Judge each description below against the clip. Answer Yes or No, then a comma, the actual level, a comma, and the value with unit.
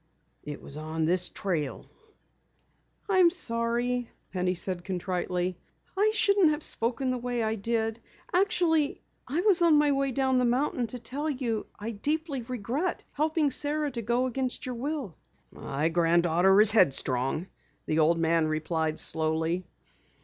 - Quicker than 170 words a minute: No, average, 150 wpm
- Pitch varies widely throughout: Yes, wide, 8.5 semitones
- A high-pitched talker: Yes, high, 230 Hz